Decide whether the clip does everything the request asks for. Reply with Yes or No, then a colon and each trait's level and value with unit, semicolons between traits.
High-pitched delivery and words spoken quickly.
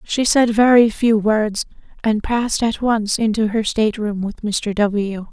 No: high, 220 Hz; average, 180 wpm